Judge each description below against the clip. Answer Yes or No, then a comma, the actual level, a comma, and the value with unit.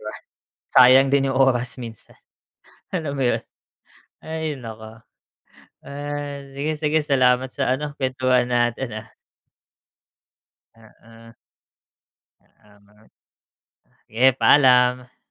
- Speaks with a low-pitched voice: Yes, low, 125 Hz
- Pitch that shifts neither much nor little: Yes, average, 3.4 semitones